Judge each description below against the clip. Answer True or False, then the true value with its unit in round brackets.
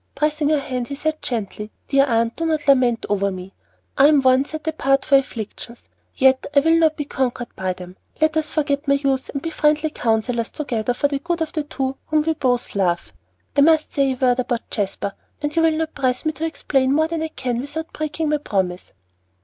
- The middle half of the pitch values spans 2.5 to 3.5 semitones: False (4.1 semitones)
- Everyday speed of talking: False (220 wpm)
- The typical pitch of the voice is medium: False (275 Hz)